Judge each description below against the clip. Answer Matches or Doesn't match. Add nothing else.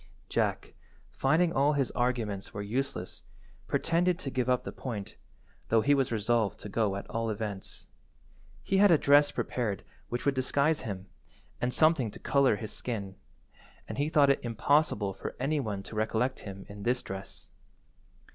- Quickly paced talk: Doesn't match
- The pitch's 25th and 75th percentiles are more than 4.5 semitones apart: Matches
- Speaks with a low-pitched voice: Matches